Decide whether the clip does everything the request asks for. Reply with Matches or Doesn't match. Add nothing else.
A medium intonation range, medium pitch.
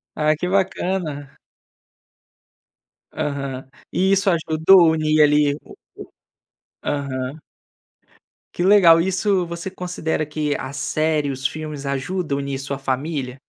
Matches